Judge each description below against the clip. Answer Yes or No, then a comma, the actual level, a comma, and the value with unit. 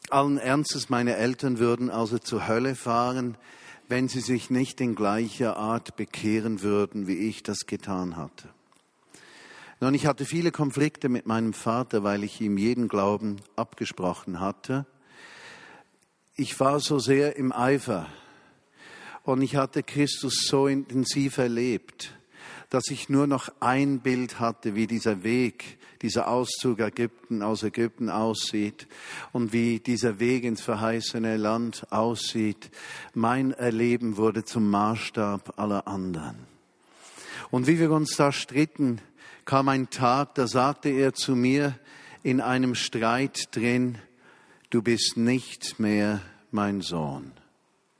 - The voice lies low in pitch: Yes, low, 120 Hz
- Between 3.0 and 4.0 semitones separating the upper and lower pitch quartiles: Yes, average, 3.5 semitones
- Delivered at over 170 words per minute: No, average, 135 wpm